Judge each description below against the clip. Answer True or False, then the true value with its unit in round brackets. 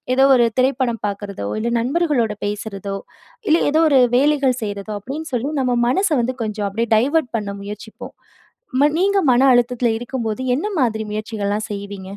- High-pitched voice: True (235 Hz)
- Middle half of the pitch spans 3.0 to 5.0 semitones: True (4.2 semitones)